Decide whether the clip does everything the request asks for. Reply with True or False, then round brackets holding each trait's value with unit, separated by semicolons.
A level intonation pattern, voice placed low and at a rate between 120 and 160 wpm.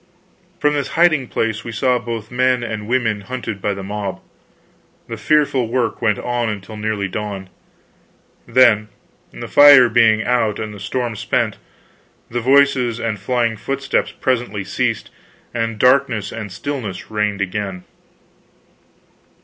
False (3.3 semitones; 115 Hz; 135 wpm)